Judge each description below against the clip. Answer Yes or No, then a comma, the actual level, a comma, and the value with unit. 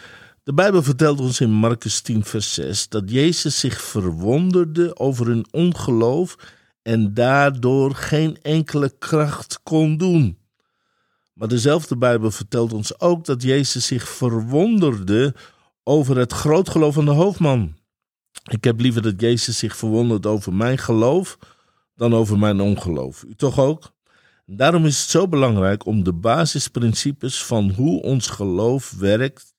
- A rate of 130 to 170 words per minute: Yes, average, 140 wpm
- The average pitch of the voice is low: Yes, low, 125 Hz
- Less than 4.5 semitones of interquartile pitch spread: No, average, 5.2 semitones